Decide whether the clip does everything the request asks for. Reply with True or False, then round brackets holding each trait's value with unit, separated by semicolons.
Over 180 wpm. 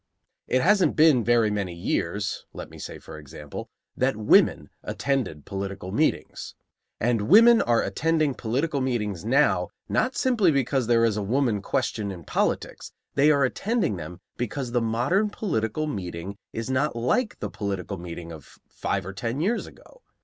False (160 wpm)